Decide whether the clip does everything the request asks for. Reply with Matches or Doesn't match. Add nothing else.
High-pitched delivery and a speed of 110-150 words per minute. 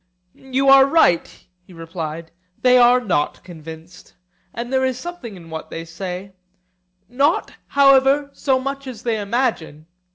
Matches